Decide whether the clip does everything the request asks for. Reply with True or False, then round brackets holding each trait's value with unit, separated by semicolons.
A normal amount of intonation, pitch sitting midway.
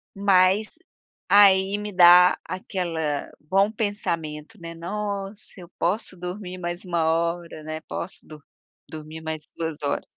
True (3.3 semitones; 180 Hz)